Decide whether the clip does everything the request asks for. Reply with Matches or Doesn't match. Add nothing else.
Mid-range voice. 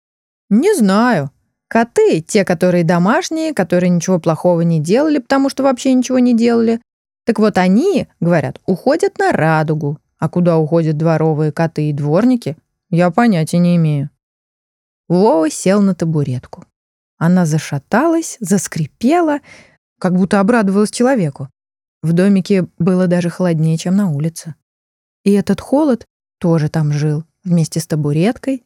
Matches